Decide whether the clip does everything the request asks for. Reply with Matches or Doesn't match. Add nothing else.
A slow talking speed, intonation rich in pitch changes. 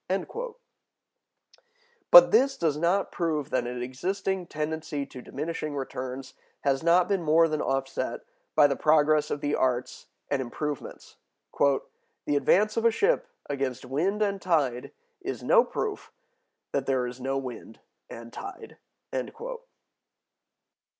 Matches